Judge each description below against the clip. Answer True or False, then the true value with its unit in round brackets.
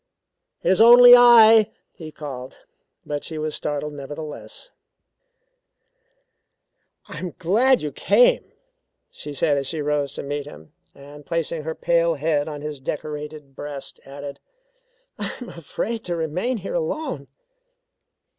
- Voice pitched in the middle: True (155 Hz)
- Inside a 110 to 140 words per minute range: True (135 wpm)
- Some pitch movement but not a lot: False (5.7 semitones)